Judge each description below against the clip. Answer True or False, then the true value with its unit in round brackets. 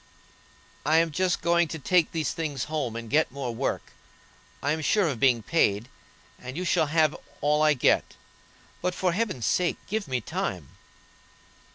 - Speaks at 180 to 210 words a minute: False (170 wpm)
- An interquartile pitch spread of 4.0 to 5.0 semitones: True (4.5 semitones)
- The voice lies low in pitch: False (155 Hz)